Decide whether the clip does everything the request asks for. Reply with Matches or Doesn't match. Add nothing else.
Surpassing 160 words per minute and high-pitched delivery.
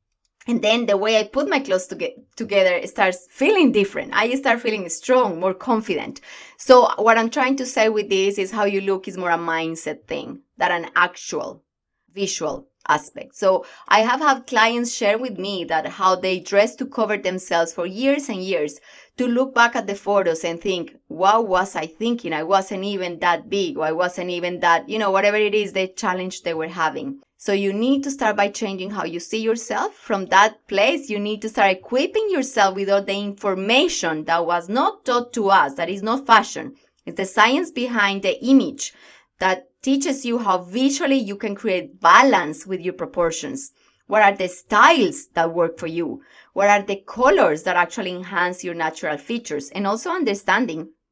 Matches